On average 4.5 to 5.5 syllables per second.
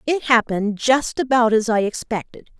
Yes: 5.0 syllables/s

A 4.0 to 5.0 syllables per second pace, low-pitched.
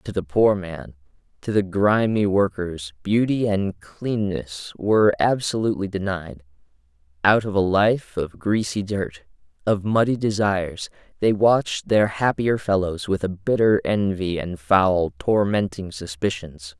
Yes: 4.1 syllables/s; low, 100 Hz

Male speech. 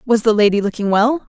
No: female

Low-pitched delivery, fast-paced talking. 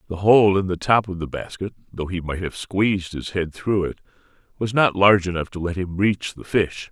Yes: very low, 95 Hz; fast, 235 wpm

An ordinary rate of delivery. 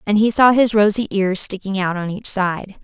No: fast, 235 wpm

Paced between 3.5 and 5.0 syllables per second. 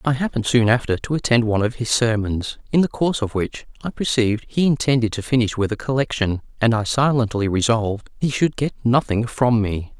No: 5.8 syllables/s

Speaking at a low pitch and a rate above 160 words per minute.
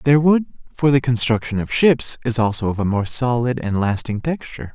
Yes: low, 120 Hz; average, 200 wpm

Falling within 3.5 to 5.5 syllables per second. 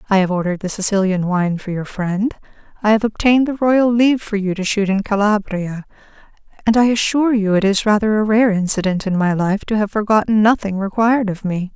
No: 5.8 syllables/s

